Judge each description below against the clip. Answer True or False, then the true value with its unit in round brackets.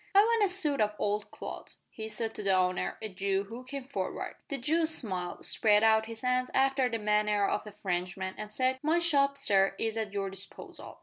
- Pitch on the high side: True (220 Hz)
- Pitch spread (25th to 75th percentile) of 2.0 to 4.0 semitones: False (5.2 semitones)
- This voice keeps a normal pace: False (210 wpm)